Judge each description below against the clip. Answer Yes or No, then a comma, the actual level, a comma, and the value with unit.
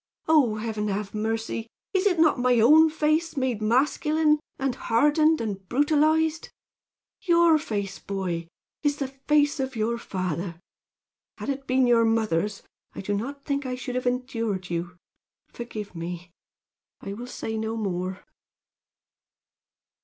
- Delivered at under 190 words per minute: Yes, average, 140 wpm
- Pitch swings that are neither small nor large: No, wide, 6.1 semitones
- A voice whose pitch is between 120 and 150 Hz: No, high, 240 Hz